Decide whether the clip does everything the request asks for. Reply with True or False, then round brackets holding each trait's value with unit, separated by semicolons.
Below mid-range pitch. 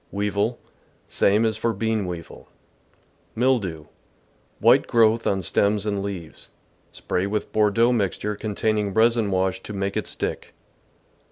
True (105 Hz)